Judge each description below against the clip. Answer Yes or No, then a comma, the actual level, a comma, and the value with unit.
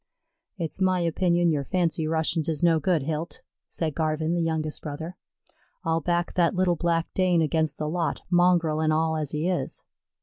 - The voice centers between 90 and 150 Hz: No, medium, 165 Hz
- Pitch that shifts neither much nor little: No, narrow, 1.8 semitones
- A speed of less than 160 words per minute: No, average, 175 wpm